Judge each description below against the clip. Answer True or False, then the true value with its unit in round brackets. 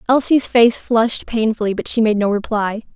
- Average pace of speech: True (185 wpm)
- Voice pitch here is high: True (225 Hz)